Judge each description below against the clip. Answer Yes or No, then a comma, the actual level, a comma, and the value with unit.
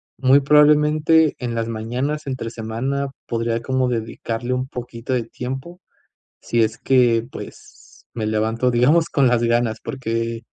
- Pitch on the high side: No, low, 125 Hz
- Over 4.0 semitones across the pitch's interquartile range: No, average, 2.9 semitones